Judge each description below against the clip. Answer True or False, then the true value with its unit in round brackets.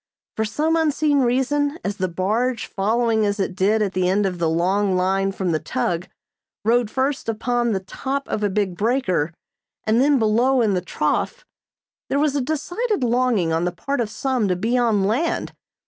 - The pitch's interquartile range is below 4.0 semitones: False (5.5 semitones)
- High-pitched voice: True (220 Hz)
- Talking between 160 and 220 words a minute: True (190 wpm)